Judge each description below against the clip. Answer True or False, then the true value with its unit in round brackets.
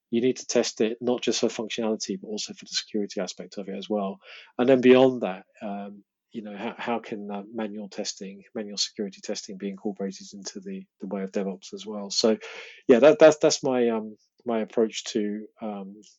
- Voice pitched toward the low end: True (110 Hz)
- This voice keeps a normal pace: False (210 wpm)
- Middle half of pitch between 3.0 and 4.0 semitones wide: True (3.3 semitones)